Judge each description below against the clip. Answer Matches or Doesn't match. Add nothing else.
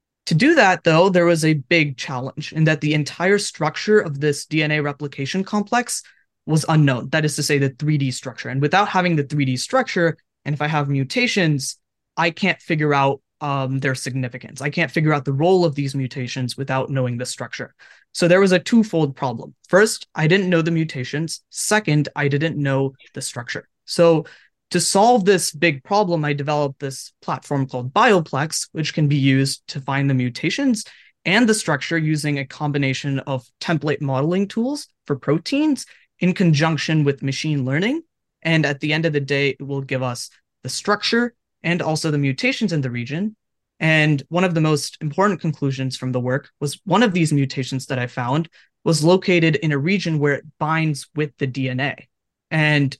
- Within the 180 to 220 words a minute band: Matches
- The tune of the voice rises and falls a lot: Doesn't match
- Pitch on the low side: Doesn't match